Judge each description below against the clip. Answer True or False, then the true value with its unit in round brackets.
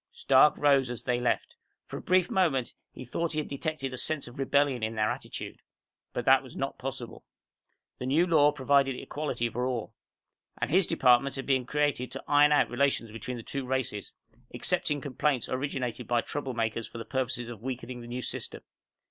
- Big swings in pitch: False (3.1 semitones)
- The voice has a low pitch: True (130 Hz)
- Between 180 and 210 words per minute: True (190 wpm)